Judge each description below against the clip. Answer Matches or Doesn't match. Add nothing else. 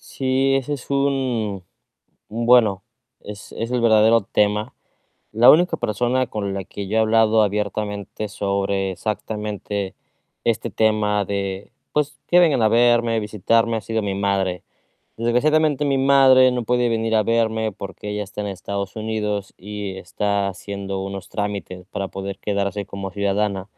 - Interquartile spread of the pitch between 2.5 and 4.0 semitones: Matches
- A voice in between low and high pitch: Doesn't match